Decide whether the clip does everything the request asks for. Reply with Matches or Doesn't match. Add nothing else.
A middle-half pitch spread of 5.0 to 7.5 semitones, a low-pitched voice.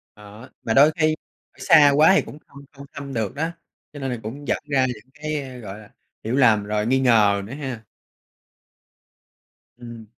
Doesn't match